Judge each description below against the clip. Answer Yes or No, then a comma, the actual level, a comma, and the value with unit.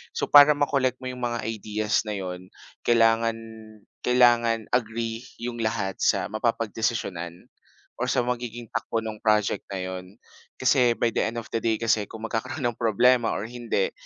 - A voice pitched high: No, low, 115 Hz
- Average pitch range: No, narrow, 2.0 semitones